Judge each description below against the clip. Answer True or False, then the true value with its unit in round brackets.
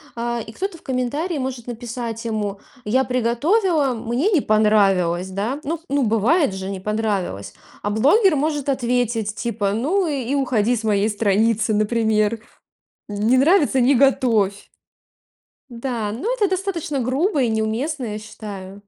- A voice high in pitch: True (235 Hz)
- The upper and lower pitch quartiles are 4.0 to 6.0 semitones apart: True (4.7 semitones)